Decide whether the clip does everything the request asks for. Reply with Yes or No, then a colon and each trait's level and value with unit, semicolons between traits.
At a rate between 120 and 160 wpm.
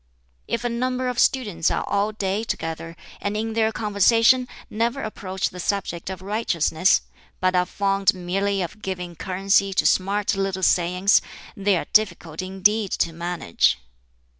Yes: average, 150 wpm